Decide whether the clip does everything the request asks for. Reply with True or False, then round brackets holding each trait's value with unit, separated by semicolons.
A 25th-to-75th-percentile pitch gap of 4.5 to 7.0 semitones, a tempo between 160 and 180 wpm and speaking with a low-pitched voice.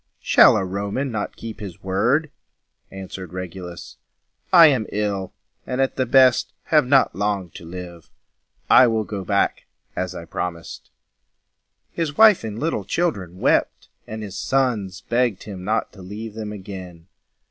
False (5.1 semitones; 150 wpm; 105 Hz)